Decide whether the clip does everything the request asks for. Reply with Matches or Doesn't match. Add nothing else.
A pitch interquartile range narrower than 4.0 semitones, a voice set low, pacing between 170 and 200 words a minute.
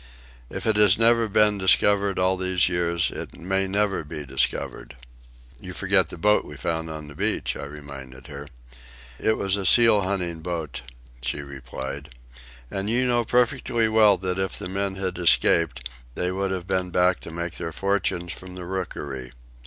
Matches